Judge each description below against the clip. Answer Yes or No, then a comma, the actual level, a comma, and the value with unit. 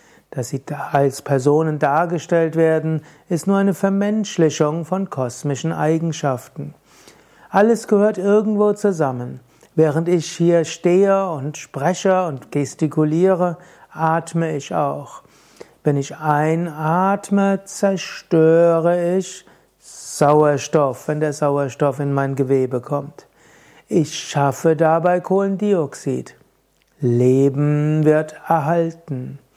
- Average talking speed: No, slow, 95 wpm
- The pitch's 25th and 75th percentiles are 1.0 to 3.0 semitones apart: No, average, 3.8 semitones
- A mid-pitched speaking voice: Yes, medium, 160 Hz